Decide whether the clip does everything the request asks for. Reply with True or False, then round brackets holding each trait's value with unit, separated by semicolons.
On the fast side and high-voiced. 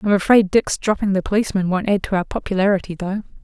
True (210 wpm; 195 Hz)